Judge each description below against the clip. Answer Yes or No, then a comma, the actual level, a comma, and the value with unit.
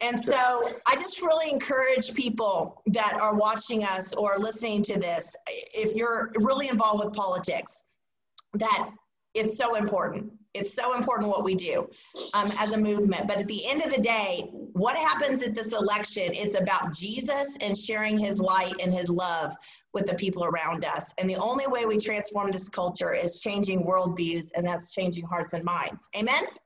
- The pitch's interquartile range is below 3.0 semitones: No, average, 3.9 semitones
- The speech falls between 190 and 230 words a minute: No, average, 180 wpm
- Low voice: No, high, 210 Hz